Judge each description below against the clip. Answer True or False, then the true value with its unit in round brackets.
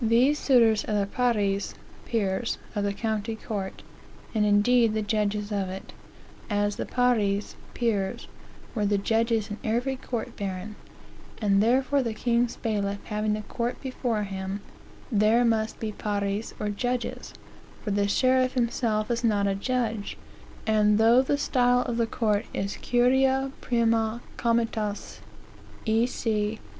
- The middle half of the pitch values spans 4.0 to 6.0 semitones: False (2.7 semitones)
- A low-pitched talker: False (220 Hz)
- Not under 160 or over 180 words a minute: False (145 wpm)